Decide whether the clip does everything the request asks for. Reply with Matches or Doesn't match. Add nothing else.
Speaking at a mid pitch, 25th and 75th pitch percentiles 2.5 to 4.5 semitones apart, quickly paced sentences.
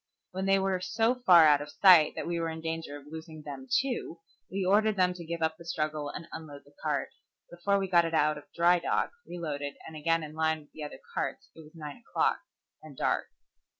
Matches